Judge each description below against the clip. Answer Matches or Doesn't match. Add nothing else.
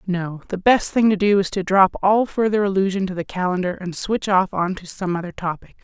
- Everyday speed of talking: Doesn't match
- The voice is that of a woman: Matches